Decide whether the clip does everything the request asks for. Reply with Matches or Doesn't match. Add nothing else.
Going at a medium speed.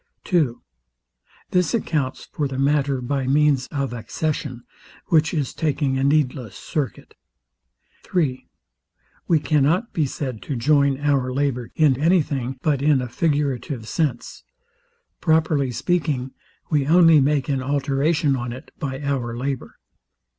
Doesn't match